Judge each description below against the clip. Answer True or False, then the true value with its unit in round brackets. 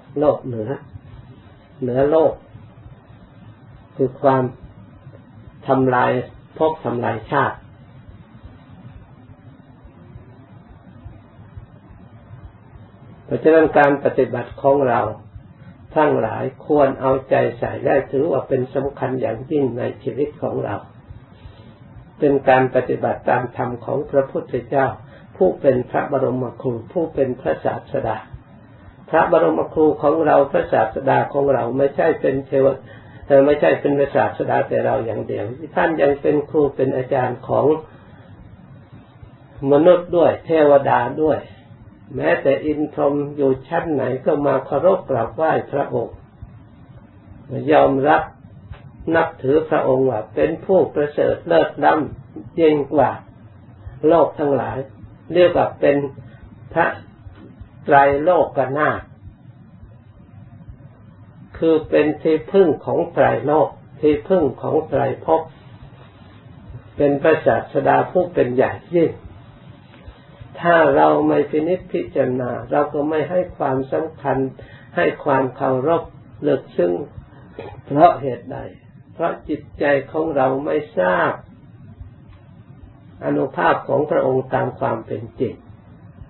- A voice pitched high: False (135 Hz)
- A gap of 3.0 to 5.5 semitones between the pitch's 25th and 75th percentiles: True (3.7 semitones)